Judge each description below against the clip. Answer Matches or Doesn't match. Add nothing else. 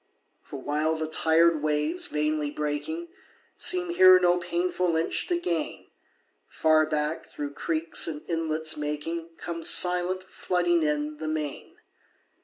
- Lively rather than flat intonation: Doesn't match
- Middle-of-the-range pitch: Matches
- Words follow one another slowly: Matches